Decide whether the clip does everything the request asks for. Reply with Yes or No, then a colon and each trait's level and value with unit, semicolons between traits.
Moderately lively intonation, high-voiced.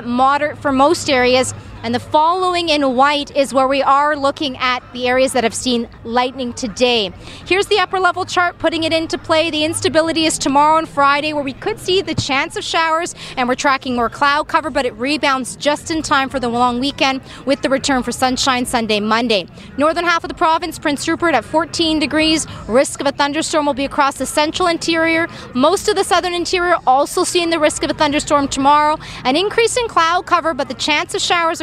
Yes: average, 3.8 semitones; very high, 300 Hz